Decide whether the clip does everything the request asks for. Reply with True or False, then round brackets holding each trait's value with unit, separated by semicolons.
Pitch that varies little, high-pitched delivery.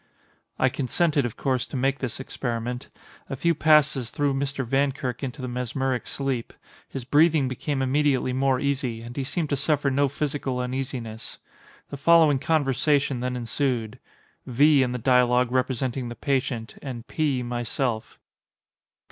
False (2.2 semitones; 130 Hz)